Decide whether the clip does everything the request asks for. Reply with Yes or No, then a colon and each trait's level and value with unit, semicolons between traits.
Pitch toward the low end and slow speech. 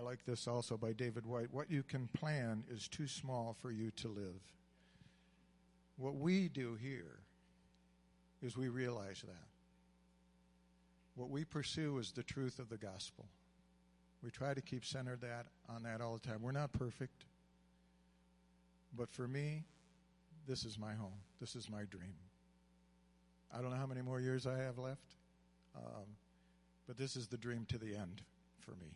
No: low, 115 Hz; average, 170 wpm